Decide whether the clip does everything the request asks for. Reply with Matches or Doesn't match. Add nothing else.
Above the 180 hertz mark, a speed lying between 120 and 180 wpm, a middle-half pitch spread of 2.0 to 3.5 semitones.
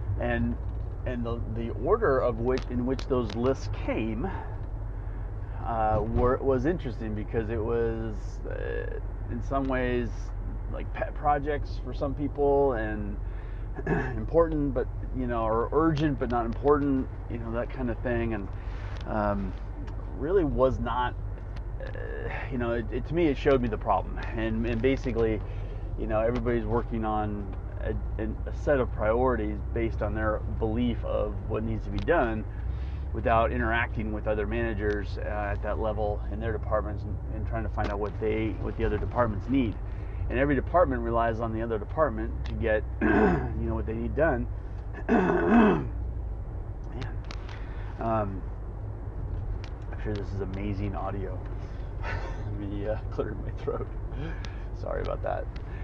Doesn't match